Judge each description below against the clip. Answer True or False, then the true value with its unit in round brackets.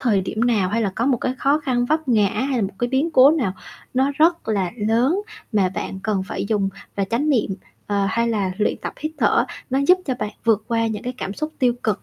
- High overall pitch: True (230 Hz)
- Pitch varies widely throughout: False (4.4 semitones)